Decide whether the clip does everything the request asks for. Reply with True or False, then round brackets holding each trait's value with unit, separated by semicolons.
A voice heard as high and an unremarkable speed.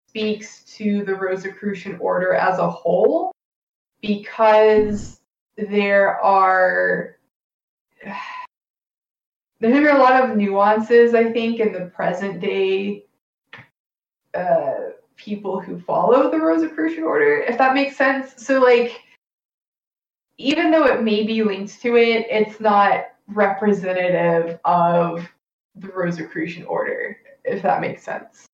False (215 Hz; 115 wpm)